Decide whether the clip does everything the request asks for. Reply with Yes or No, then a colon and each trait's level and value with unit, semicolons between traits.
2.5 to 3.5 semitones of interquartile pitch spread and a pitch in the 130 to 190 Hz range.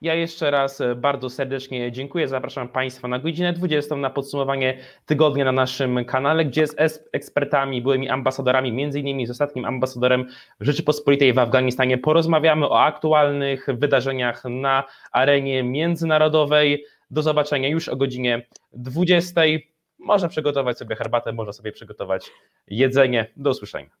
Yes: average, 2.9 semitones; low, 135 Hz